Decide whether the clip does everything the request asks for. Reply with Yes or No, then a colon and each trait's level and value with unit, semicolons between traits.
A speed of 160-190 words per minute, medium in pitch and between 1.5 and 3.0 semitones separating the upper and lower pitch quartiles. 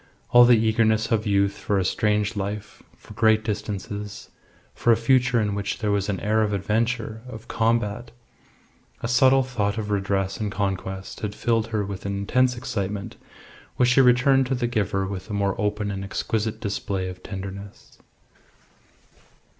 No: average, 165 wpm; low, 105 Hz; narrow, 2.6 semitones